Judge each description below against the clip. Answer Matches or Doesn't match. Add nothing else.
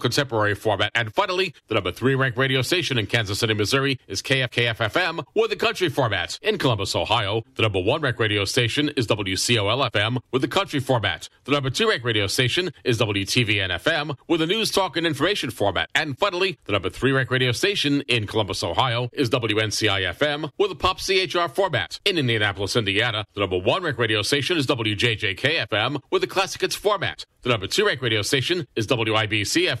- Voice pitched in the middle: Doesn't match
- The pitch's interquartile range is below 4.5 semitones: Doesn't match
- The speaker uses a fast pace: Doesn't match